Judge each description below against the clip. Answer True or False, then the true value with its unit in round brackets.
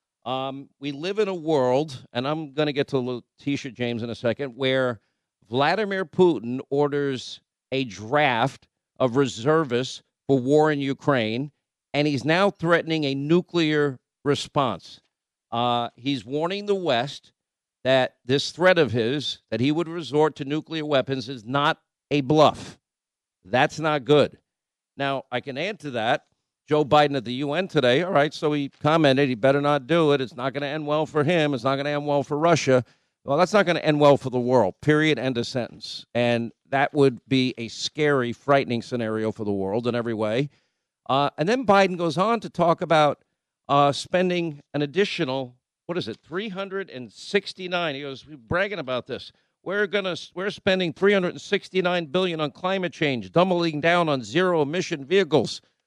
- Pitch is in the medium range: True (145 Hz)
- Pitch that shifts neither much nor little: True (4.3 semitones)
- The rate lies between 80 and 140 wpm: False (185 wpm)